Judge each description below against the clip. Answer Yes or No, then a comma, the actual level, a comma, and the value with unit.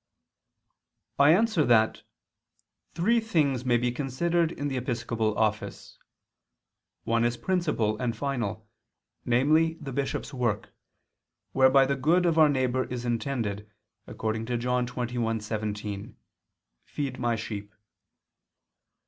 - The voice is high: No, low, 125 Hz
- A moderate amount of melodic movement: Yes, average, 4.0 semitones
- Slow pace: Yes, slow, 115 wpm